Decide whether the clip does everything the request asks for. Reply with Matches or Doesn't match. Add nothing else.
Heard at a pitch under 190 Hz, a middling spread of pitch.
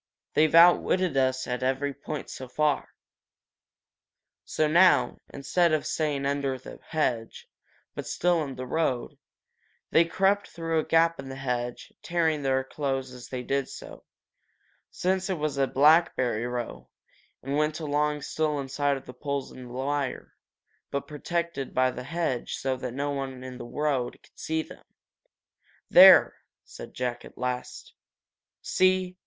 Matches